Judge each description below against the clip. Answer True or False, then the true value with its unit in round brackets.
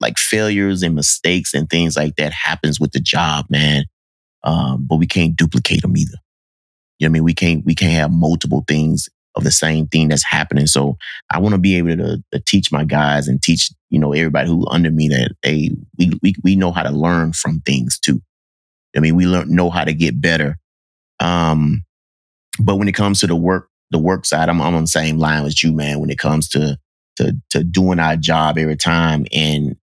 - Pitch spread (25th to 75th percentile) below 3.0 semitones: True (2.5 semitones)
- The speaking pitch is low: True (80 Hz)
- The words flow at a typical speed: False (225 wpm)